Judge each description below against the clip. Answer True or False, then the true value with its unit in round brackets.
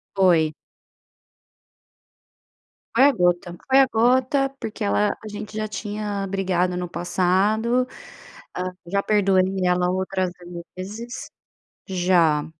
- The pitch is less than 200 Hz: True (190 Hz)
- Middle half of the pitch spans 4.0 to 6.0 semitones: False (3.3 semitones)